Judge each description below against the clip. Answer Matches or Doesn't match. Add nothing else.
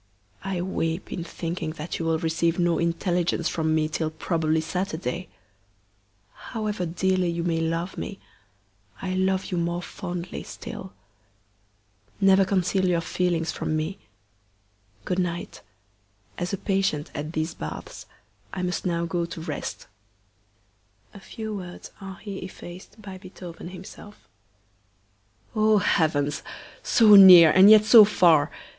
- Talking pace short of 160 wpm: Matches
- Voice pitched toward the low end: Doesn't match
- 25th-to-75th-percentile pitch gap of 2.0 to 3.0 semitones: Matches